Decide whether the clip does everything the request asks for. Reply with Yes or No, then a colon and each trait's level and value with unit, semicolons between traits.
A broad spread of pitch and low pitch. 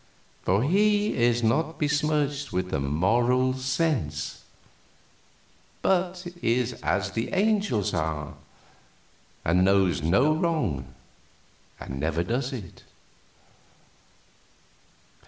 Yes: wide, 8.9 semitones; low, 120 Hz